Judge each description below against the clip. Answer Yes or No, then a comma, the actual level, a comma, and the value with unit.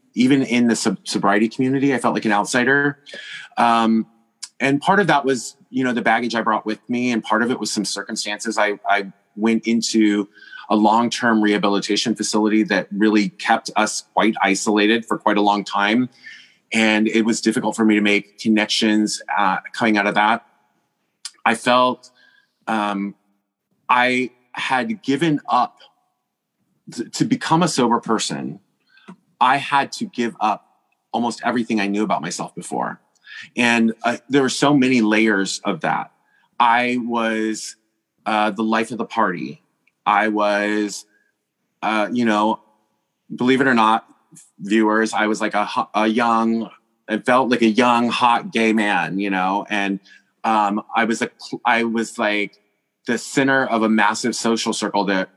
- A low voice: Yes, low, 110 Hz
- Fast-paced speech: No, average, 160 wpm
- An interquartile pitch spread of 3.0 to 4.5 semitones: No, narrow, 2.5 semitones